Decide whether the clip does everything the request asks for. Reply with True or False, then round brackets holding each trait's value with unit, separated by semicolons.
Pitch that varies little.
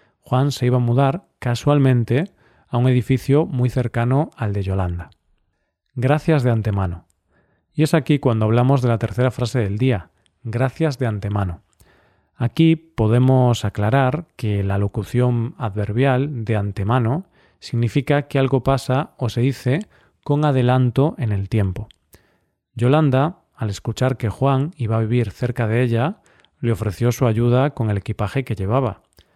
False (3.7 semitones)